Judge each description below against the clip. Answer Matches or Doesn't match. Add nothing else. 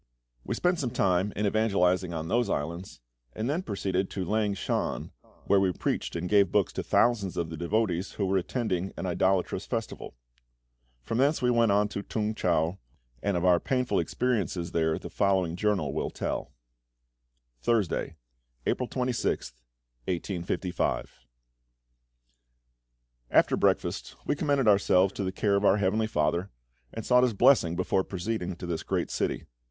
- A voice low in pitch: Matches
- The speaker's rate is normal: Matches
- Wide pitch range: Doesn't match